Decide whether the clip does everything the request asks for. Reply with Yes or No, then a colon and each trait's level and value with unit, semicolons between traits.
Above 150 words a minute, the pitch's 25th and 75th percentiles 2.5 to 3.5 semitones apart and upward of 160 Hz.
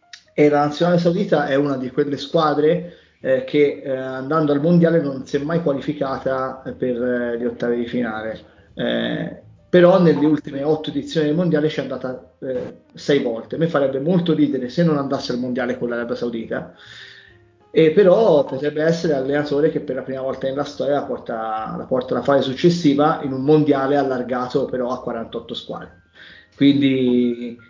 No: fast, 170 wpm; average, 2.9 semitones; medium, 140 Hz